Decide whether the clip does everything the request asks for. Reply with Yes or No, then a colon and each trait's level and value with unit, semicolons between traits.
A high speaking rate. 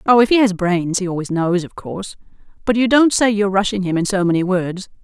Yes: fast, 250 wpm